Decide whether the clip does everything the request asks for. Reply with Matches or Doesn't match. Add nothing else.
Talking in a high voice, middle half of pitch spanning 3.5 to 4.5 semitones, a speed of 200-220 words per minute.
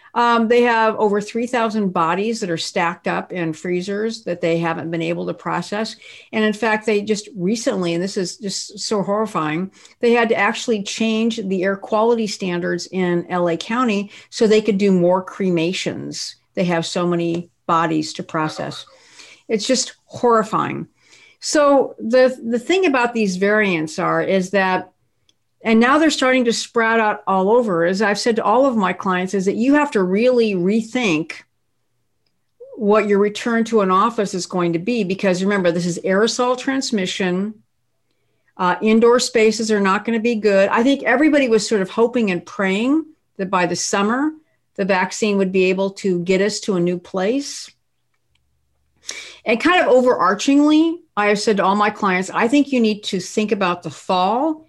Doesn't match